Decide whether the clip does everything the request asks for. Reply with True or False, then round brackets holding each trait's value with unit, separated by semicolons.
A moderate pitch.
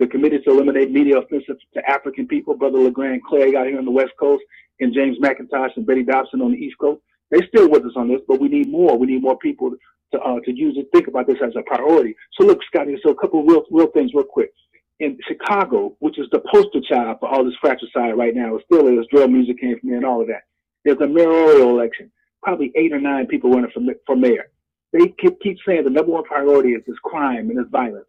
True (150 Hz)